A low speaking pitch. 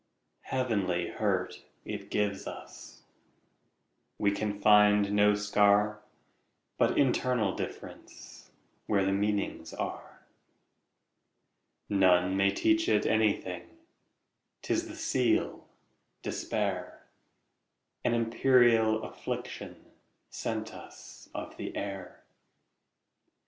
Yes: low, 105 Hz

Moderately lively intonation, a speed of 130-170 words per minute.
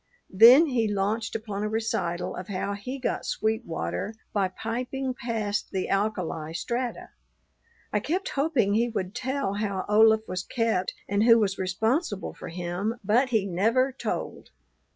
Yes: average, 3.6 semitones; average, 155 wpm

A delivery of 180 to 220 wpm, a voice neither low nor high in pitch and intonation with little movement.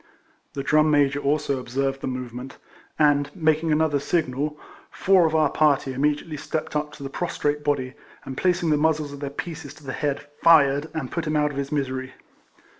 Yes: average, 190 wpm; medium, 145 Hz; narrow, 2.1 semitones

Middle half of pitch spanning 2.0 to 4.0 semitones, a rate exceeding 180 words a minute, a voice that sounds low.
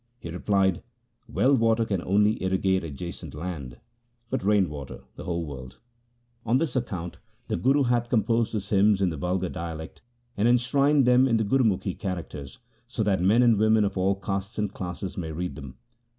No: average, 4.6 semitones; average, 195 wpm; low, 100 Hz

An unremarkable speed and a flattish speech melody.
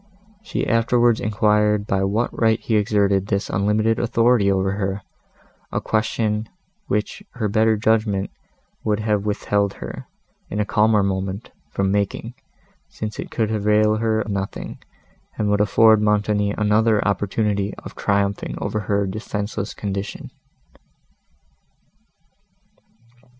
No: slow, 120 wpm; narrow, 1.5 semitones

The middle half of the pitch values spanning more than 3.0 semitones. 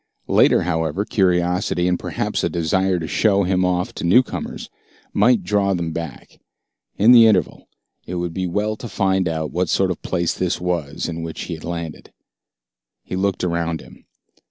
No: narrow, 2.5 semitones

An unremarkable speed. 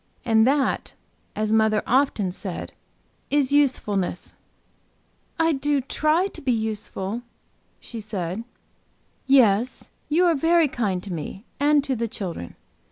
No: slow, 125 wpm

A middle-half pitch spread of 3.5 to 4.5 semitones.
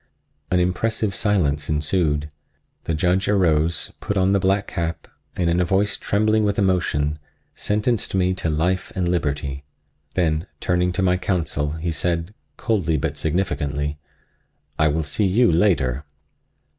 Yes: average, 3.9 semitones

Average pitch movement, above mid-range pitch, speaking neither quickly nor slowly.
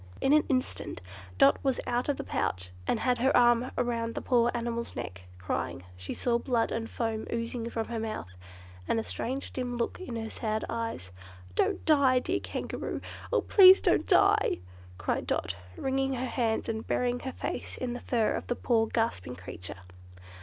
No: narrow, 2.3 semitones; high, 235 Hz; average, 185 wpm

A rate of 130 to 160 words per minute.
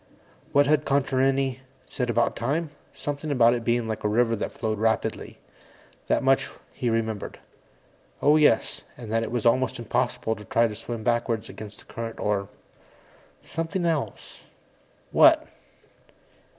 Yes: average, 150 wpm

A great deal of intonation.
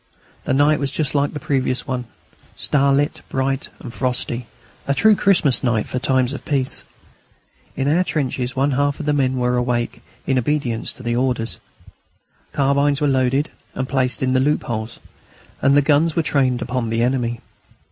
No: narrow, 2.4 semitones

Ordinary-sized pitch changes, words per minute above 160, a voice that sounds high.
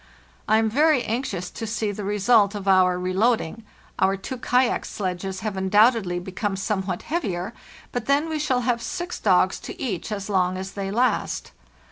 Yes: average, 4.0 semitones; average, 170 wpm; high, 210 Hz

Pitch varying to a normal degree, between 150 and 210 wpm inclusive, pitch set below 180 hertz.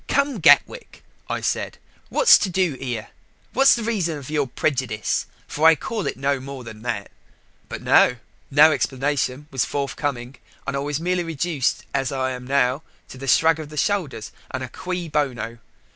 Yes: average, 4.1 semitones; average, 180 wpm; medium, 140 Hz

